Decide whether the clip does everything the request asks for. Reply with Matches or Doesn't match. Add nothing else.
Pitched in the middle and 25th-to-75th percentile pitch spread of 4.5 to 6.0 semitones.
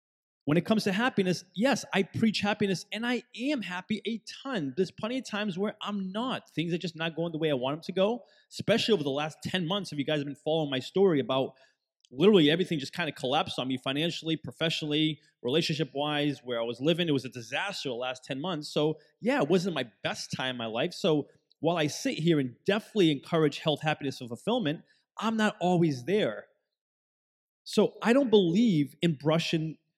Matches